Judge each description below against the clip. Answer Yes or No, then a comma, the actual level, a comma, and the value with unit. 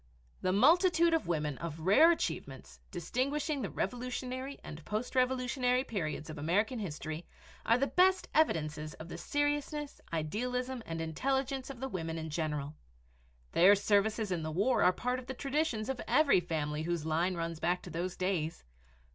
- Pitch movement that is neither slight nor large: No, wide, 8.2 semitones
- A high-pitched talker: Yes, high, 205 Hz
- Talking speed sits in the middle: Yes, average, 165 wpm